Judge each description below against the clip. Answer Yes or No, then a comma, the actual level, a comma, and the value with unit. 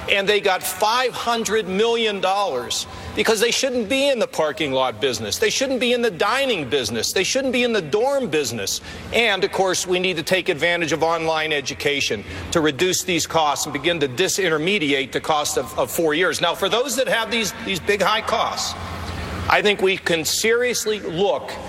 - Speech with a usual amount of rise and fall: No, wide, 6.7 semitones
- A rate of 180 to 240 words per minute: Yes, average, 195 wpm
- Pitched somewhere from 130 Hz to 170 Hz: No, medium, 185 Hz